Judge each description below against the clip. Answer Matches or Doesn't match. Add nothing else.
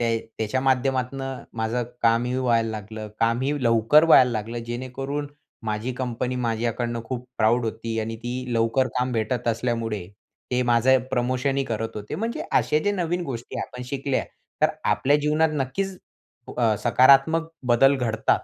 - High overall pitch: Doesn't match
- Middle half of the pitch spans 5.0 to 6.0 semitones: Doesn't match